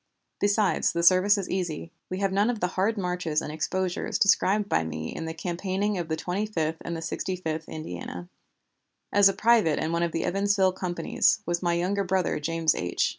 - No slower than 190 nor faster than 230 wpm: Yes, average, 195 wpm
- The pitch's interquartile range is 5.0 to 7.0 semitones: No, average, 3.3 semitones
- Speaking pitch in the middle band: Yes, medium, 180 Hz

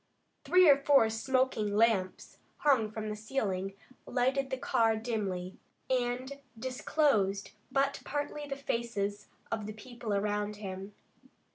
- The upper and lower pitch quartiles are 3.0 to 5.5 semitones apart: Yes, average, 4.4 semitones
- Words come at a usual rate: No, slow, 125 wpm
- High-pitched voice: Yes, high, 225 Hz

